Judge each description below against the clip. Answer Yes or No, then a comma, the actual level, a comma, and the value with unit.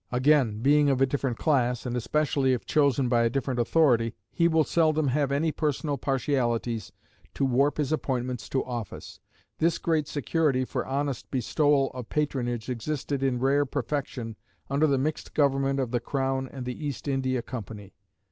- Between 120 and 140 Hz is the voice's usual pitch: Yes, low, 135 Hz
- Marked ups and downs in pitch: No, average, 2.9 semitones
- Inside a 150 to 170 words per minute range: Yes, average, 165 wpm